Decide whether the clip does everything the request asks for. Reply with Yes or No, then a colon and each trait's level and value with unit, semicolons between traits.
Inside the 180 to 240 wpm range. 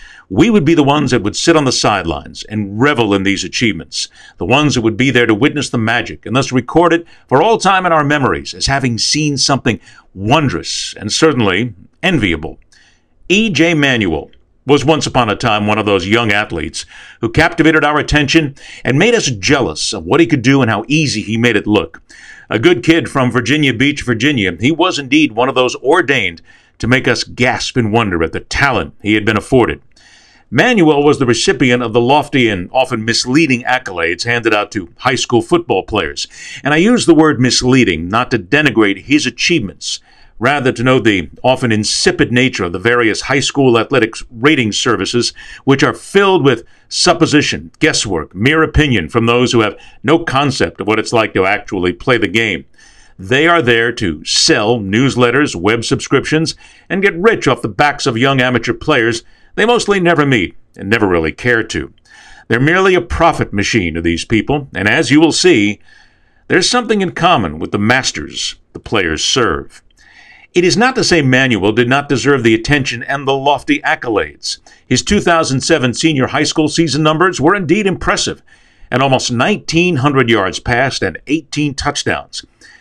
Yes: average, 185 wpm